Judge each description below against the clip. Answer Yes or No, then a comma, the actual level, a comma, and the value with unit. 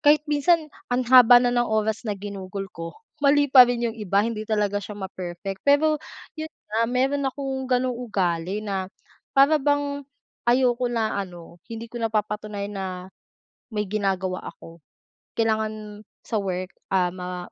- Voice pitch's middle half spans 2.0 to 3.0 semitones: No, average, 4.5 semitones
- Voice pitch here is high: Yes, high, 220 Hz